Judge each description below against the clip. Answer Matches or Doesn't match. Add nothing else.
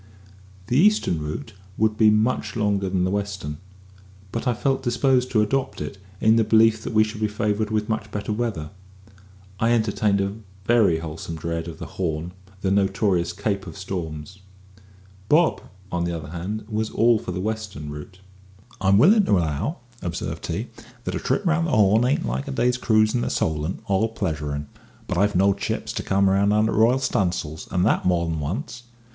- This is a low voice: Matches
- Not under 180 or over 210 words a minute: Matches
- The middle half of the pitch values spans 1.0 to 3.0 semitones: Doesn't match